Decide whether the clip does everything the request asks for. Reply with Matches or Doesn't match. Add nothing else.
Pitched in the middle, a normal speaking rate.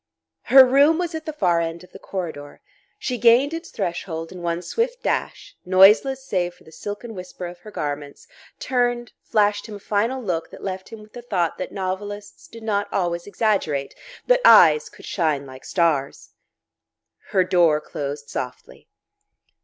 Doesn't match